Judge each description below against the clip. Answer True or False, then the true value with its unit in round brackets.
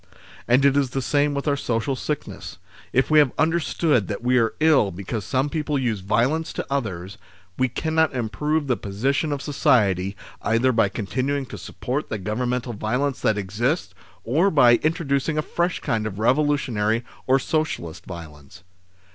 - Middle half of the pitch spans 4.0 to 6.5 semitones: True (5.2 semitones)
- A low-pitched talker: True (125 Hz)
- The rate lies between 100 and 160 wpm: False (170 wpm)